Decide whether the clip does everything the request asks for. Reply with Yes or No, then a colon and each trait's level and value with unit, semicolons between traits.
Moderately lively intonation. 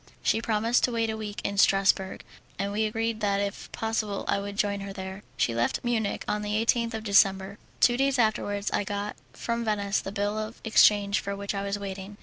No: narrow, 1.8 semitones